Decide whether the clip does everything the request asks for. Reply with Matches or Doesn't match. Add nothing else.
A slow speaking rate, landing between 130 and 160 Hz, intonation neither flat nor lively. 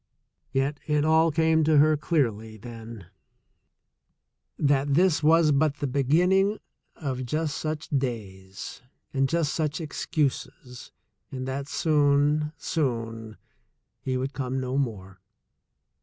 Matches